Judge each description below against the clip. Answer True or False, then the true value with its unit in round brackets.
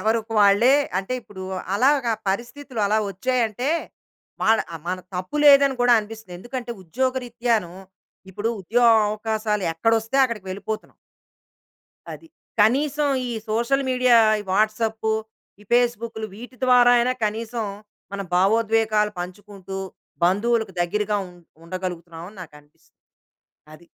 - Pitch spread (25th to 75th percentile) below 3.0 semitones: False (3.5 semitones)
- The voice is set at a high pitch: True (220 Hz)